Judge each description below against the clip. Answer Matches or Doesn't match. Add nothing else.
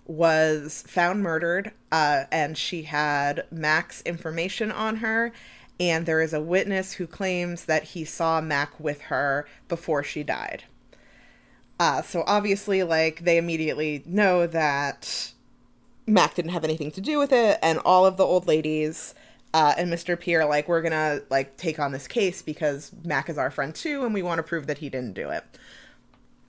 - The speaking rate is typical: Matches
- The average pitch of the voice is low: Doesn't match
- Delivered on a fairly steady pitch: Doesn't match